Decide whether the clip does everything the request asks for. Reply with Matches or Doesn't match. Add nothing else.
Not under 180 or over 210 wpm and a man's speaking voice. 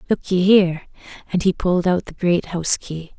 Doesn't match